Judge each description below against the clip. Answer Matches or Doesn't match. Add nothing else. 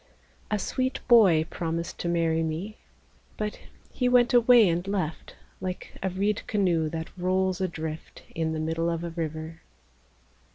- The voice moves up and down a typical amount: Matches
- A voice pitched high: Doesn't match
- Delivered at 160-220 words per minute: Doesn't match